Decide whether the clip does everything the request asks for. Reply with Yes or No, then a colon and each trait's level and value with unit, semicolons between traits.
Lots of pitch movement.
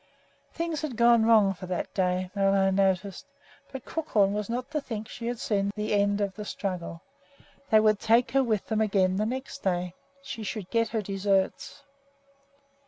No: average, 3.1 semitones